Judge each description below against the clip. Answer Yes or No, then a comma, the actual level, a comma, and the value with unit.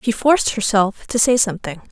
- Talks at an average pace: Yes, average, 190 wpm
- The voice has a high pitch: Yes, high, 220 Hz